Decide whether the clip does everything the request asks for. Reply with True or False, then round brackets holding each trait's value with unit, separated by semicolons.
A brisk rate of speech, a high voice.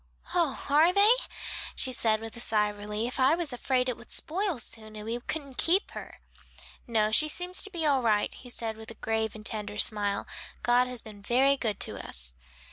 True (210 wpm; 235 Hz)